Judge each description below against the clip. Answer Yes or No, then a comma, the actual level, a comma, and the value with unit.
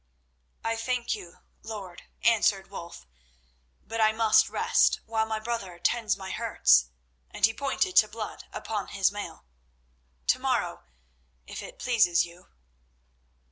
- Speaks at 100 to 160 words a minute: Yes, slow, 135 wpm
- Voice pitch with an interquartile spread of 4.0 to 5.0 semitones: No, average, 3.3 semitones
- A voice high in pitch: Yes, high, 215 Hz